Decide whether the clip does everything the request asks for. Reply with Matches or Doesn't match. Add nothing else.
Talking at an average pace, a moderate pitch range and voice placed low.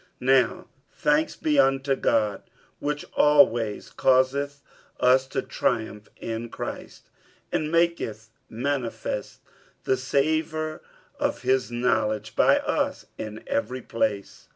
Doesn't match